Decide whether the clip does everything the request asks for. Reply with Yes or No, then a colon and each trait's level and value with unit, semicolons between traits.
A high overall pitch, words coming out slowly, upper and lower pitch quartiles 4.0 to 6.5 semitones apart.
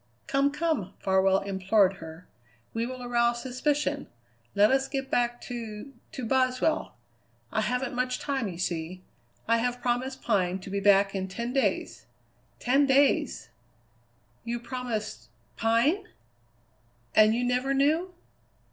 Yes: high, 240 Hz; slow, 130 wpm; average, 4.9 semitones